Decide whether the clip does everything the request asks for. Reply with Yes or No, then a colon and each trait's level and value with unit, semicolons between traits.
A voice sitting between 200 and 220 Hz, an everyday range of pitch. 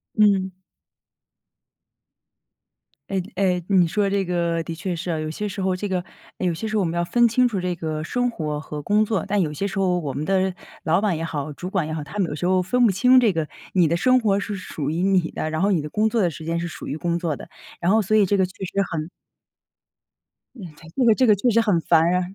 No: medium, 185 Hz; average, 3.8 semitones